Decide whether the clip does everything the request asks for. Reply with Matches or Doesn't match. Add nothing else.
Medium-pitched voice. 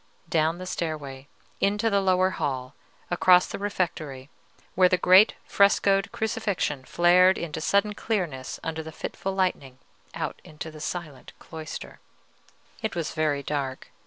Matches